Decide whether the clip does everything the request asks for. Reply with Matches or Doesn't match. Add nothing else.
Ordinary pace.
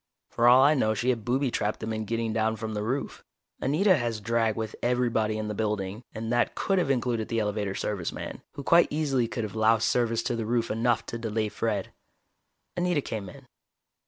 Doesn't match